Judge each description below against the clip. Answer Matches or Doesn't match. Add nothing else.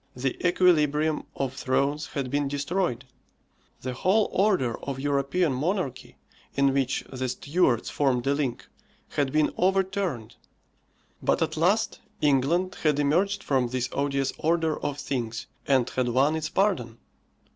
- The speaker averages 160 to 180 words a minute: Doesn't match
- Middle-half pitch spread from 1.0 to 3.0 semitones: Doesn't match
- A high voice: Doesn't match